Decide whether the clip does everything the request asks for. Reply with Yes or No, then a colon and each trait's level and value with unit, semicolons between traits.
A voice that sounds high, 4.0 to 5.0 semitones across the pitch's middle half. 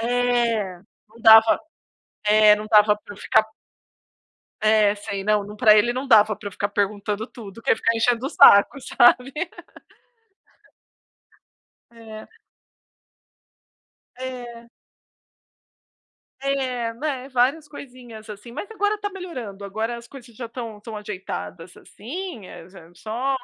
No: high, 230 Hz; average, 3.2 semitones